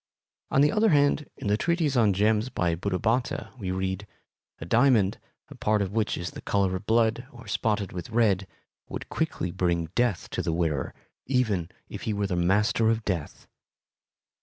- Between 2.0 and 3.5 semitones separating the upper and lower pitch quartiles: No, average, 4.2 semitones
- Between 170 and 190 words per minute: Yes, average, 180 wpm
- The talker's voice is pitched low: Yes, low, 105 Hz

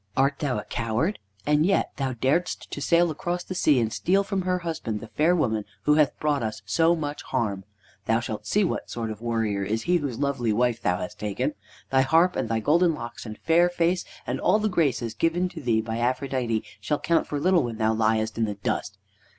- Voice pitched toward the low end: Yes, low, 130 Hz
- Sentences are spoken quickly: Yes, fast, 220 wpm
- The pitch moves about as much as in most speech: No, wide, 7.0 semitones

